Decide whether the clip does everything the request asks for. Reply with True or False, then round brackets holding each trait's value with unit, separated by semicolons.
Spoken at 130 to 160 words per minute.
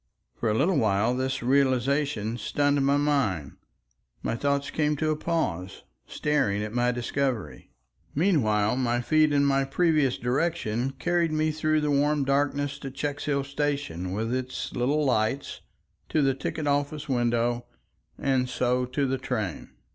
True (145 wpm)